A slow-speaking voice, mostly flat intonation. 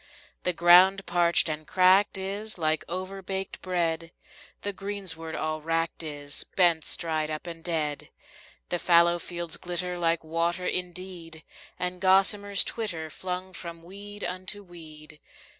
Yes: slow, 130 wpm; narrow, 2.3 semitones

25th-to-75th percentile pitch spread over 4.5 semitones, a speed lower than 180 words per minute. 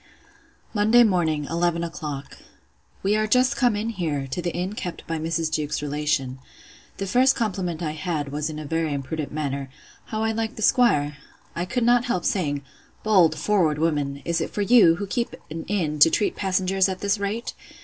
No: wide, 5.4 semitones; average, 185 wpm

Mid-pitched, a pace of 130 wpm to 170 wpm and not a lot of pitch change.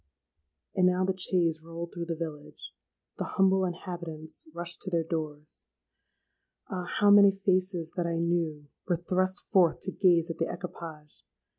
Yes: medium, 170 Hz; average, 150 wpm; narrow, 2.3 semitones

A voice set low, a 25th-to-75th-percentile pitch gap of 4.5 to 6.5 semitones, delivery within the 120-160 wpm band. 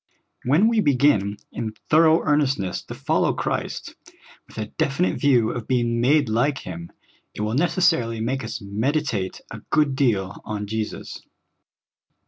Yes: low, 125 Hz; average, 5.3 semitones; average, 140 wpm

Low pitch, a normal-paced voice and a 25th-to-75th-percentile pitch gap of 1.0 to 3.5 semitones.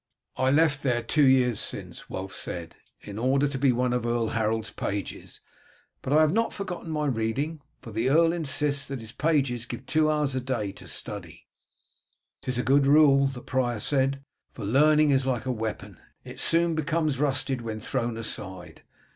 No: low, 130 Hz; average, 180 wpm; average, 4.1 semitones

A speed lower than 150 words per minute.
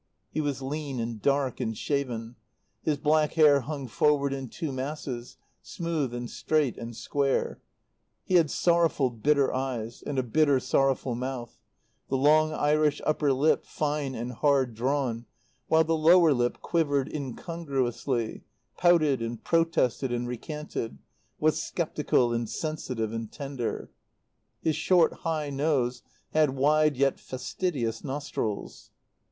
Yes: slow, 135 wpm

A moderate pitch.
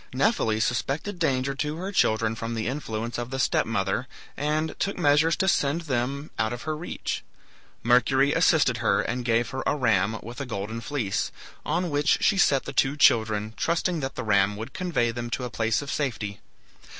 No: low, 130 Hz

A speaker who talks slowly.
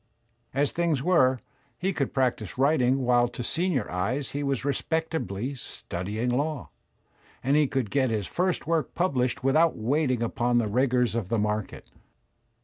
No: average, 155 wpm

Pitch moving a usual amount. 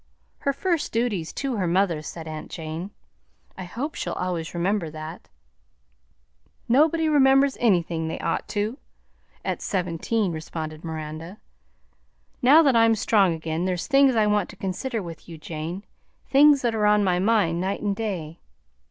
No: wide, 5.8 semitones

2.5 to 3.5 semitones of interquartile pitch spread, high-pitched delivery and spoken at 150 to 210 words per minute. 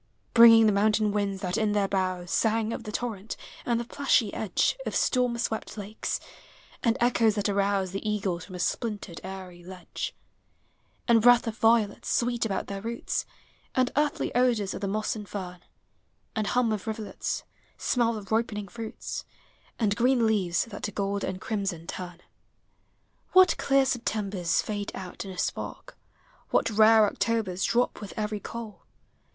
Yes: average, 2.8 semitones; high, 215 Hz; average, 165 wpm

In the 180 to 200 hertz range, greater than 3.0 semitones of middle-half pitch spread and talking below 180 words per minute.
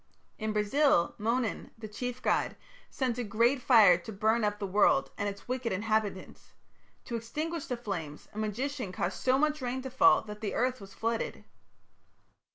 No: high, 225 Hz; average, 3.6 semitones; average, 170 wpm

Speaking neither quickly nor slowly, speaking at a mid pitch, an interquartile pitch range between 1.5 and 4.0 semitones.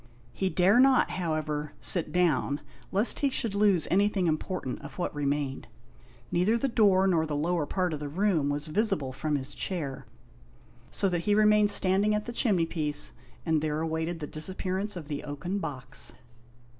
No: average, 170 wpm; medium, 175 Hz; average, 5.0 semitones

